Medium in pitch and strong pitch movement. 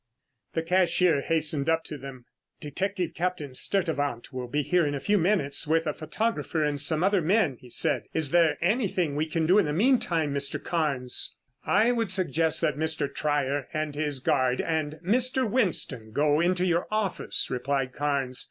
No: medium, 160 Hz; average, 4.1 semitones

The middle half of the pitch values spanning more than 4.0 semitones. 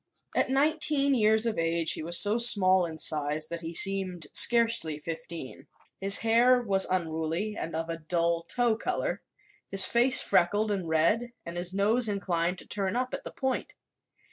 Yes: wide, 5.6 semitones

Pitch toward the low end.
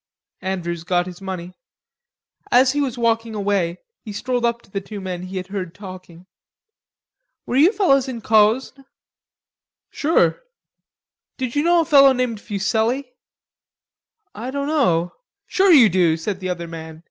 No: high, 215 Hz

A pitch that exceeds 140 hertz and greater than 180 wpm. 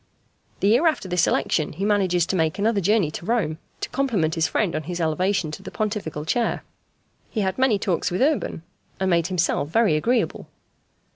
Yes: high, 190 Hz; average, 190 wpm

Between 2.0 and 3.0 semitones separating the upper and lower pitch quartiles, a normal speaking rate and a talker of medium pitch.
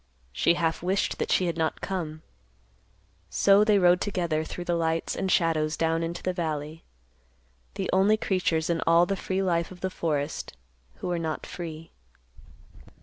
Yes: narrow, 2.4 semitones; average, 165 wpm; medium, 170 Hz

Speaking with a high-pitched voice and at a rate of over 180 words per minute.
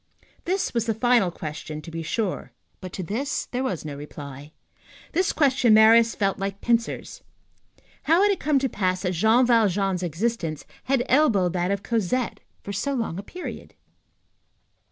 No: high, 215 Hz; average, 165 wpm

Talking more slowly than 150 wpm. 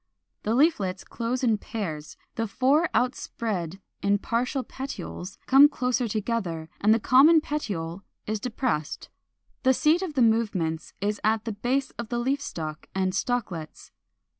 Yes: average, 140 wpm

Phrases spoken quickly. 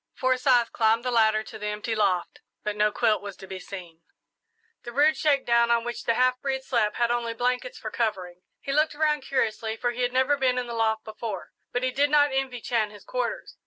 Yes: fast, 220 wpm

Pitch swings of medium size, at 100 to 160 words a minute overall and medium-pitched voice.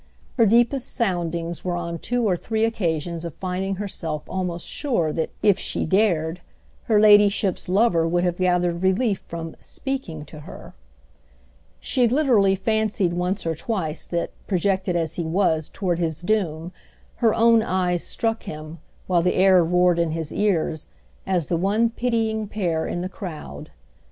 Yes: average, 4.0 semitones; average, 155 wpm; medium, 180 Hz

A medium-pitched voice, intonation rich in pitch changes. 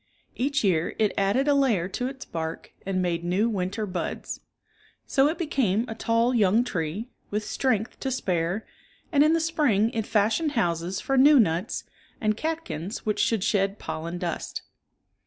No: high, 215 Hz; wide, 6.2 semitones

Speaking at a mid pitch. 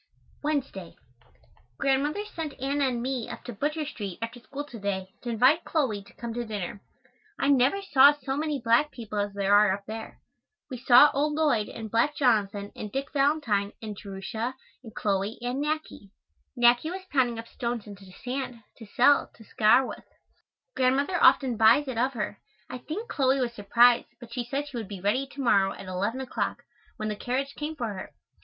No: high, 245 Hz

